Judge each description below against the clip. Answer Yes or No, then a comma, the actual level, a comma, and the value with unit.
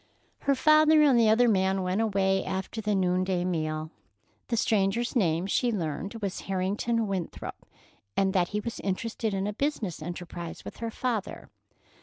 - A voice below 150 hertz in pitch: No, high, 195 Hz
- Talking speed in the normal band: Yes, average, 160 wpm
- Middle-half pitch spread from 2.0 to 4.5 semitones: Yes, average, 3.9 semitones